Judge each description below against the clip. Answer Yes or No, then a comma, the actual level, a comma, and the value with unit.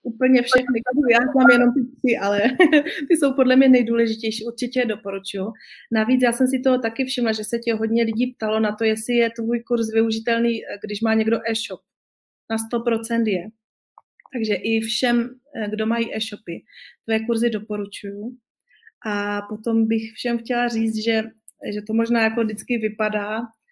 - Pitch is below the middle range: No, high, 230 Hz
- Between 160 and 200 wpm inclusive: Yes, average, 165 wpm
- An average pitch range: No, narrow, 1.9 semitones